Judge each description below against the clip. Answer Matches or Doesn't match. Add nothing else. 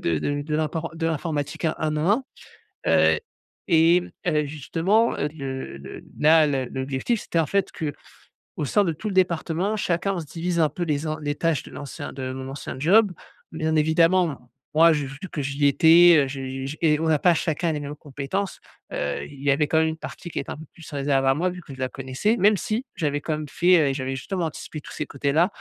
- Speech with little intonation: Doesn't match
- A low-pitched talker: Doesn't match